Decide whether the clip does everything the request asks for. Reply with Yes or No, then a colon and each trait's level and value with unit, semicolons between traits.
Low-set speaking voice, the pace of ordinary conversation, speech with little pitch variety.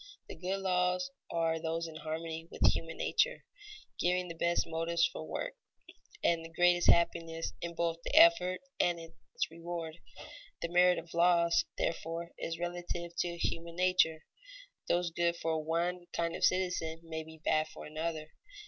No: medium, 170 Hz; average, 160 wpm; narrow, 1.3 semitones